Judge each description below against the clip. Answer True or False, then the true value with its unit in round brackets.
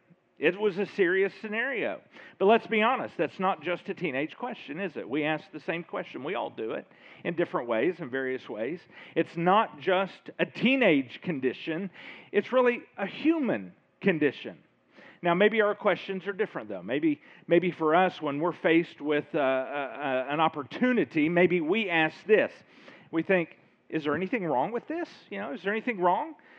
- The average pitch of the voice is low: False (180 Hz)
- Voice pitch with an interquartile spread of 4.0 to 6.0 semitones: True (5.2 semitones)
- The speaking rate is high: False (185 wpm)